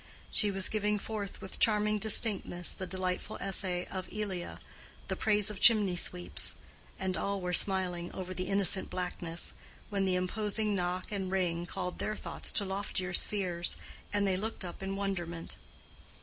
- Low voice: No, high, 190 Hz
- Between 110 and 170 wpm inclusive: Yes, average, 160 wpm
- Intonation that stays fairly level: Yes, narrow, 2.2 semitones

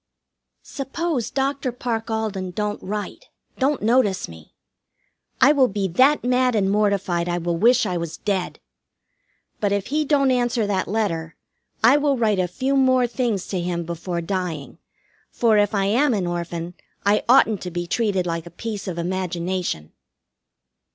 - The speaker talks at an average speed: Yes, average, 160 wpm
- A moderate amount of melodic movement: No, wide, 5.8 semitones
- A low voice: No, high, 205 Hz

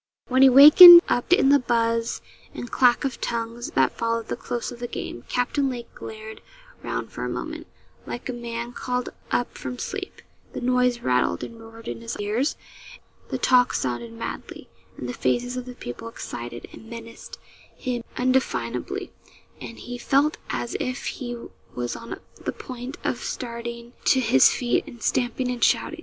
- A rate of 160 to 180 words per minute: Yes, average, 170 wpm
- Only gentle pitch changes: Yes, narrow, 1.7 semitones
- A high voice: Yes, high, 240 Hz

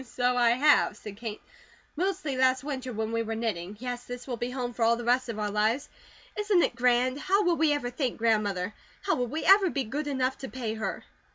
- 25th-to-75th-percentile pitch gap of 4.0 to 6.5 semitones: No, average, 3.6 semitones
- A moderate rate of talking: No, fast, 225 wpm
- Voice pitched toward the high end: Yes, high, 245 Hz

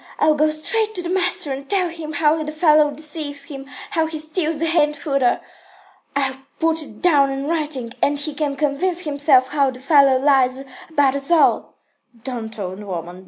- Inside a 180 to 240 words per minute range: Yes, average, 190 wpm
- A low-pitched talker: No, very high, 295 Hz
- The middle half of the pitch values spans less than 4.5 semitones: Yes, average, 2.7 semitones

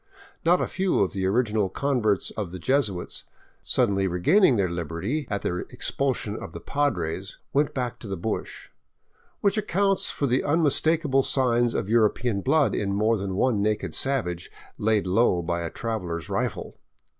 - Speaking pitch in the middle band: No, low, 110 Hz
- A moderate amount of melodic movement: No, wide, 6.3 semitones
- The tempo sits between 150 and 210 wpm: Yes, average, 170 wpm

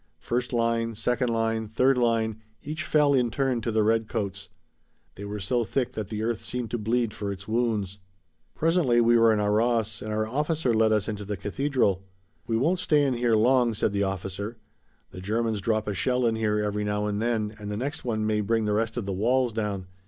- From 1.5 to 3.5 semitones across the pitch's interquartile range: Yes, narrow, 2.6 semitones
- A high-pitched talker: No, low, 115 Hz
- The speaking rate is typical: No, fast, 210 wpm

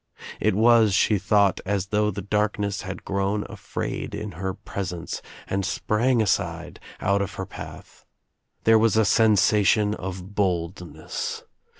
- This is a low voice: Yes, low, 100 Hz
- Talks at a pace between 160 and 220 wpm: No, slow, 135 wpm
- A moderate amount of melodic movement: No, narrow, 2.0 semitones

